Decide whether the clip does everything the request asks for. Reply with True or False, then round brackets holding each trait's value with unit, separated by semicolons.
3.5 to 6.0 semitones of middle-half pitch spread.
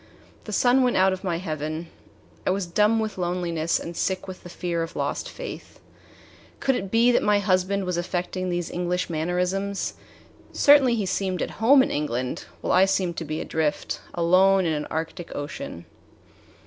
False (2.8 semitones)